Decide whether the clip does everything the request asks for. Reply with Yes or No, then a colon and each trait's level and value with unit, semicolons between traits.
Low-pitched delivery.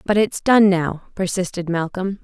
No: high, 190 Hz